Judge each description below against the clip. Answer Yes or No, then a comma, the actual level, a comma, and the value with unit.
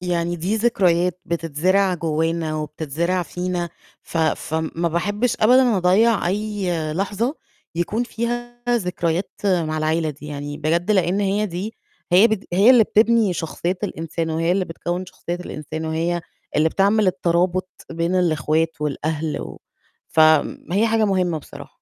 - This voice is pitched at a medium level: Yes, medium, 175 Hz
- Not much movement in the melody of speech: No, average, 3.7 semitones